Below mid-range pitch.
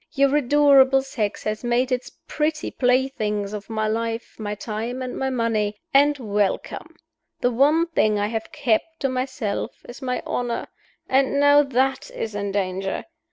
No: high, 245 Hz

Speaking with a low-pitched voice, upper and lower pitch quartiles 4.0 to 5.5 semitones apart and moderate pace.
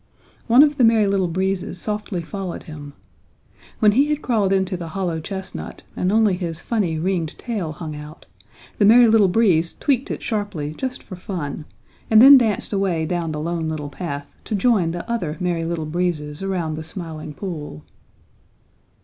No: medium, 180 Hz; average, 4.7 semitones; average, 175 wpm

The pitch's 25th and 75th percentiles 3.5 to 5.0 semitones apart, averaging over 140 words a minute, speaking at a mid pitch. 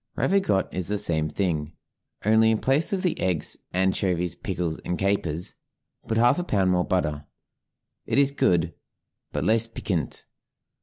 No: average, 4.7 semitones; average, 150 wpm; very low, 95 Hz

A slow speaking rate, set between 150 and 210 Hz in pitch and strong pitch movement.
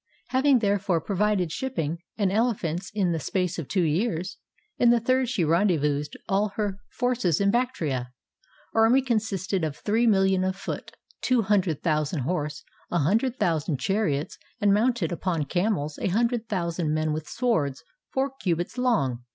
No: average, 160 wpm; high, 190 Hz; wide, 5.7 semitones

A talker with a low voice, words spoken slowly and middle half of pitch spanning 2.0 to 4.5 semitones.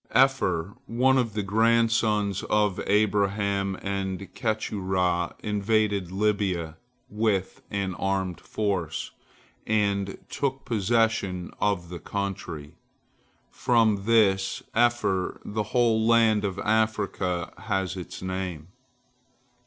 Yes: low, 100 Hz; slow, 100 wpm; average, 2.7 semitones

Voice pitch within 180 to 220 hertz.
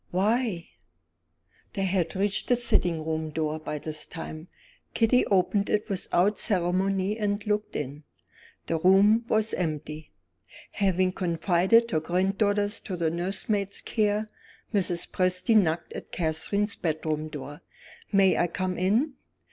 Yes: medium, 185 Hz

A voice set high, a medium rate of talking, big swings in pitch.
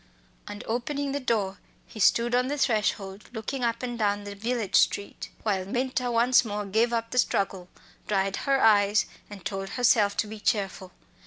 No: high, 220 Hz; average, 175 wpm; average, 3.3 semitones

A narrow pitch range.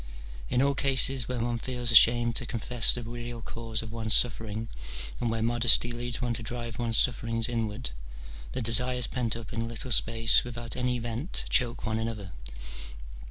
Yes: narrow, 1.3 semitones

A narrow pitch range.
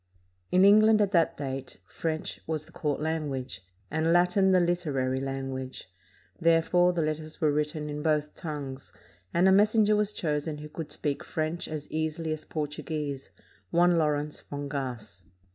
No: average, 3.0 semitones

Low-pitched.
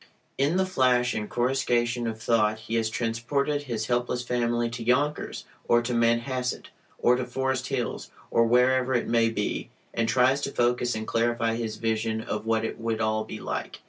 Yes: low, 120 Hz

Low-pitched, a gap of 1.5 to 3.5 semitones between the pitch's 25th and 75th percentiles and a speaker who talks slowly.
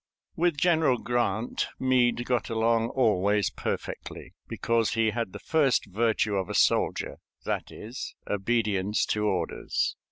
Yes: low, 115 Hz; average, 2.9 semitones; slow, 130 wpm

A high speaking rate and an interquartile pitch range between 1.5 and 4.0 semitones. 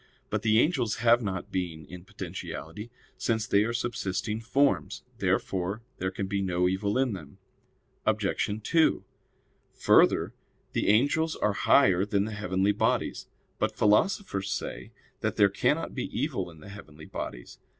No: average, 150 wpm; average, 3.5 semitones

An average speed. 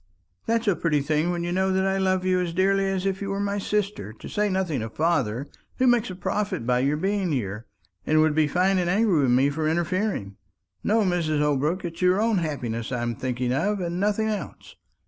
No: fast, 220 wpm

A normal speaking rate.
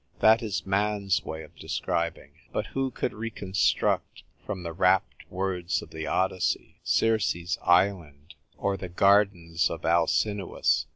No: slow, 130 wpm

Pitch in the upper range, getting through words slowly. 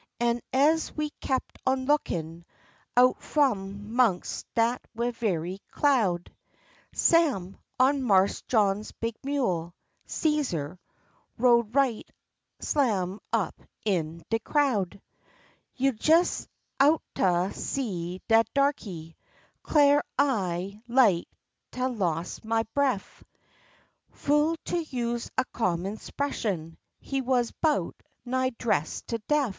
Yes: high, 235 Hz; slow, 105 wpm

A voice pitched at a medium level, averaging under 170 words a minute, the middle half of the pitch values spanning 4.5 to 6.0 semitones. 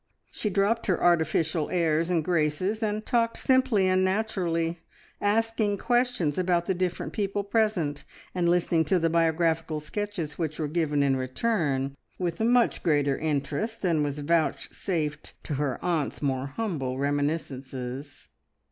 Yes: medium, 170 Hz; average, 140 wpm; average, 5.3 semitones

